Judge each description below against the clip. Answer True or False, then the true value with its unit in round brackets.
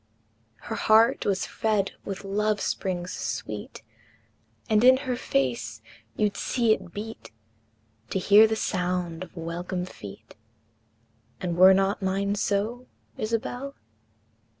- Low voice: False (200 Hz)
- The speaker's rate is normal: False (120 wpm)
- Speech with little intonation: False (3.4 semitones)